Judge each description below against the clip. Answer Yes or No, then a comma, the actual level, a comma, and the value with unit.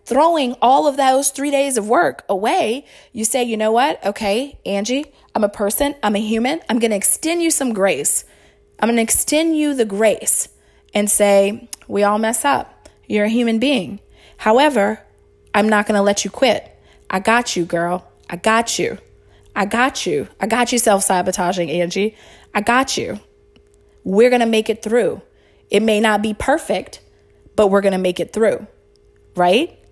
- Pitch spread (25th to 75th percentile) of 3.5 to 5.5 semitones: Yes, average, 4.1 semitones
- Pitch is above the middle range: Yes, high, 220 Hz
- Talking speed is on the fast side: No, average, 185 wpm